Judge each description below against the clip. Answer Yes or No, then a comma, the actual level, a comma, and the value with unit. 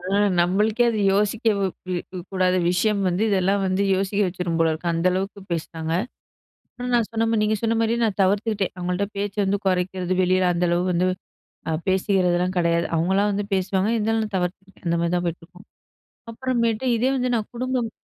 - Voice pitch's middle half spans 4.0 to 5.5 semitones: No, average, 3.2 semitones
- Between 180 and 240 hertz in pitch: Yes, high, 190 Hz